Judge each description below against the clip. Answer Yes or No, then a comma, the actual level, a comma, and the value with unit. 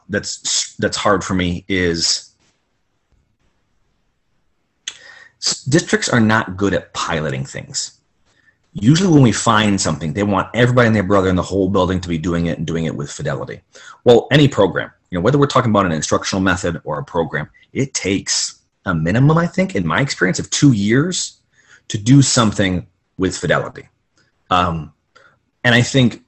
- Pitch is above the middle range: No, low, 100 Hz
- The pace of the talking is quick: No, average, 165 wpm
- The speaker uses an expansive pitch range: Yes, wide, 5.9 semitones